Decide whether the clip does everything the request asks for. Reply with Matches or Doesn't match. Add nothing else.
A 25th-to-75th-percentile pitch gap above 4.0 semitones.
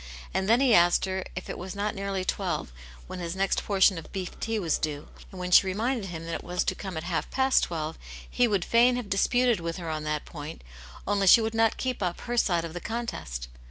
Matches